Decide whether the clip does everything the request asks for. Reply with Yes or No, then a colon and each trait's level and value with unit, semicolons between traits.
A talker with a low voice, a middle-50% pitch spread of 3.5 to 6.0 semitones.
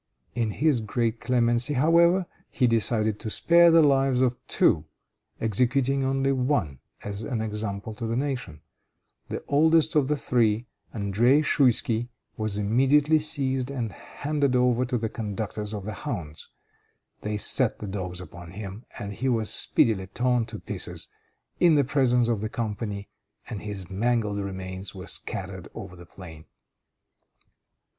Yes: low, 115 Hz; average, 4.6 semitones